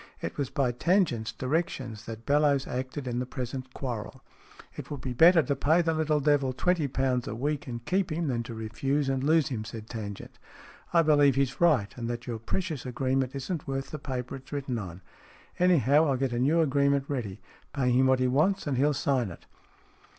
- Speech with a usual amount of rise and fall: Yes, average, 3.3 semitones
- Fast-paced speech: Yes, fast, 210 wpm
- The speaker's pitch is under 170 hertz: Yes, low, 135 Hz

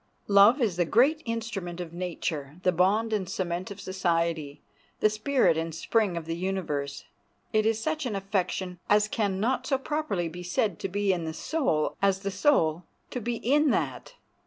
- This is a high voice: Yes, high, 195 Hz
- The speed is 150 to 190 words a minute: Yes, average, 180 wpm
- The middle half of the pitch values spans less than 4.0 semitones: No, average, 4.5 semitones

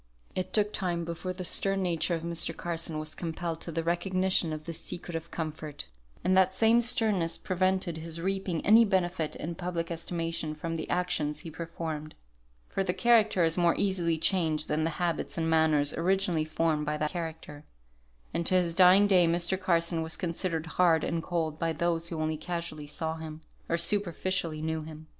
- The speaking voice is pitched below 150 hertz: No, medium, 170 Hz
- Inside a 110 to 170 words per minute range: No, average, 185 wpm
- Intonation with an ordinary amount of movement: No, narrow, 2.3 semitones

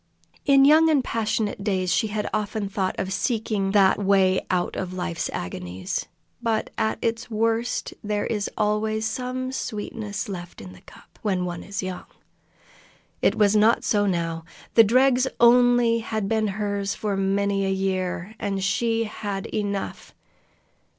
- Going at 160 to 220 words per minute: No, average, 150 wpm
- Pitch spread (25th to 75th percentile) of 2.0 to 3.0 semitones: Yes, average, 2.7 semitones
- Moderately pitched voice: No, high, 205 Hz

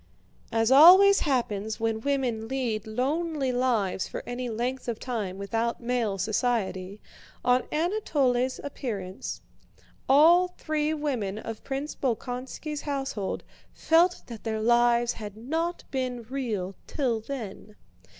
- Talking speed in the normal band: No, slow, 120 wpm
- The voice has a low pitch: No, high, 245 Hz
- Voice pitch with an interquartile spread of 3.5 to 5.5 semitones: Yes, average, 4.2 semitones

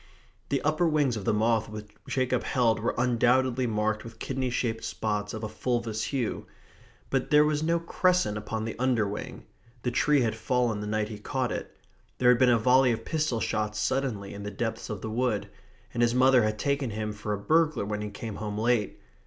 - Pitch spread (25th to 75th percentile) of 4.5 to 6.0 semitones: No, average, 3.4 semitones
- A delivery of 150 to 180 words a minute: No, fast, 205 wpm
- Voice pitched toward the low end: Yes, low, 115 Hz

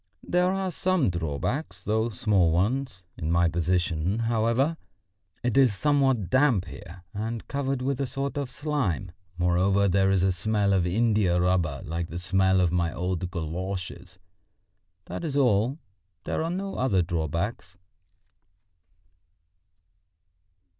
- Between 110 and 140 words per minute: Yes, slow, 135 wpm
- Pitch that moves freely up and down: Yes, wide, 6.7 semitones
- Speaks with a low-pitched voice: Yes, low, 100 Hz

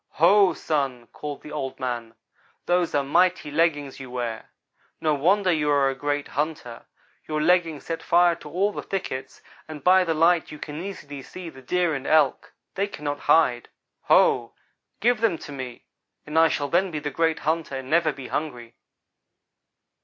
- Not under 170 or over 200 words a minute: Yes, average, 175 wpm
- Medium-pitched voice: Yes, medium, 150 Hz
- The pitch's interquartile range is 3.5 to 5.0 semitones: Yes, average, 3.9 semitones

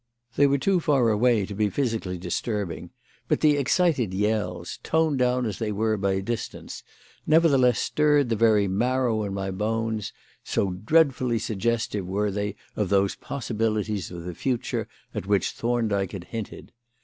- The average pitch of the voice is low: Yes, low, 110 Hz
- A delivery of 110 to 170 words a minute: Yes, average, 155 wpm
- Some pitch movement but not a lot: Yes, average, 4.1 semitones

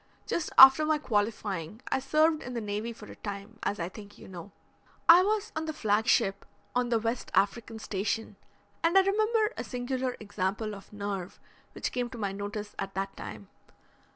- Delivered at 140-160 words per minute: No, average, 185 wpm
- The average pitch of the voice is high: Yes, high, 220 Hz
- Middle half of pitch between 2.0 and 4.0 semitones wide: No, average, 4.8 semitones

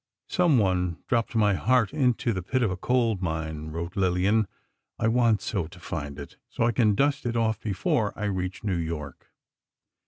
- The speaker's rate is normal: Yes, average, 180 wpm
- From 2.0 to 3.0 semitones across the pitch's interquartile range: No, average, 4.8 semitones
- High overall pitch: No, low, 105 Hz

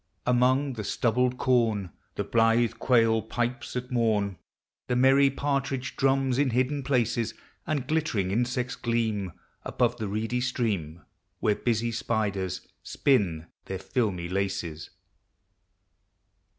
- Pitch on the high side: No, low, 120 Hz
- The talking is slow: Yes, slow, 115 wpm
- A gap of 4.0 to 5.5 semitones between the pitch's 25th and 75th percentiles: No, average, 3.5 semitones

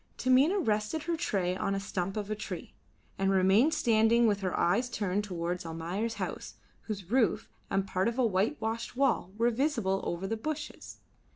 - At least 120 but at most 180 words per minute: Yes, average, 175 wpm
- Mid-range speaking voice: No, high, 210 Hz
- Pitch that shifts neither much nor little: Yes, average, 3.9 semitones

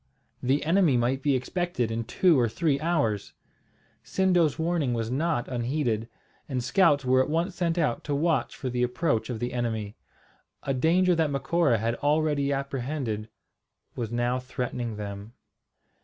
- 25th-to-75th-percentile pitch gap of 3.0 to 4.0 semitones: No, average, 4.9 semitones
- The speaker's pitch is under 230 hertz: Yes, low, 135 Hz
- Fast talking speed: No, average, 155 wpm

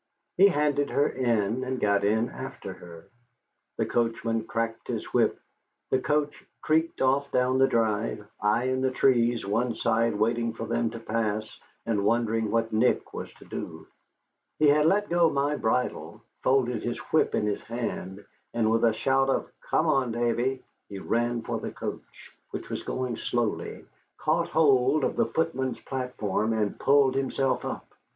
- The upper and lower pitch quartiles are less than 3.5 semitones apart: Yes, average, 3.0 semitones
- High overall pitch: No, low, 120 Hz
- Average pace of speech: Yes, average, 165 wpm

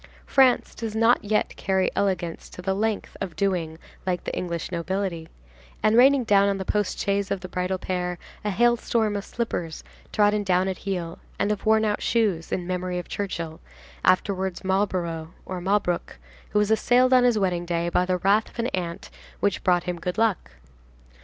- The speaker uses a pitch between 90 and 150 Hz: No, high, 190 Hz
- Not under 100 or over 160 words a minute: No, average, 185 wpm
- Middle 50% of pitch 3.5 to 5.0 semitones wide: No, average, 2.9 semitones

